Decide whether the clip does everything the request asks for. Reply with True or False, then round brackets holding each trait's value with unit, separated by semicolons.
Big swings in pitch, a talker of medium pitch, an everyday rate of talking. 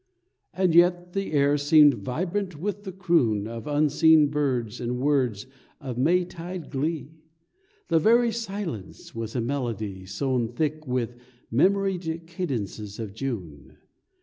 False (6.7 semitones; 145 Hz; 130 wpm)